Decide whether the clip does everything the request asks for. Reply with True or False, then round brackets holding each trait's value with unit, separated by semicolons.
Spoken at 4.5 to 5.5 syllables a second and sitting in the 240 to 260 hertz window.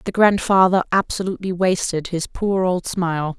False (5.0 syllables/s; 185 Hz)